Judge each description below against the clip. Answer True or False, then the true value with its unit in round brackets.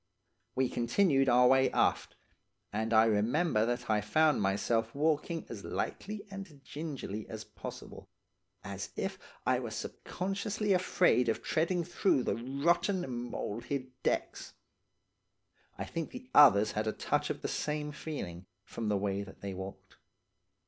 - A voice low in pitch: True (130 Hz)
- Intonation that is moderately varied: False (7.1 semitones)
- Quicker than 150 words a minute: False (145 wpm)